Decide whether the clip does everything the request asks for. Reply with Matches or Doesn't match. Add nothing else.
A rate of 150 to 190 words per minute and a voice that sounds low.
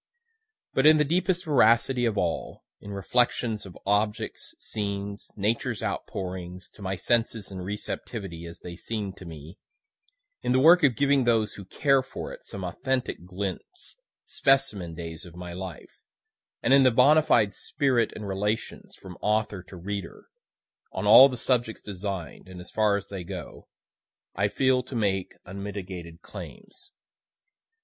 Matches